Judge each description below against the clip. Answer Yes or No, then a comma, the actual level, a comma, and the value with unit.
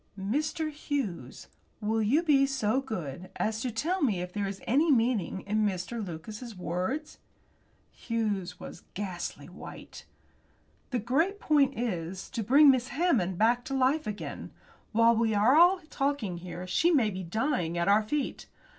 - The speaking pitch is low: No, high, 225 Hz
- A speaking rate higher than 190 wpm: No, average, 155 wpm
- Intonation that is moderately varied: No, wide, 6.2 semitones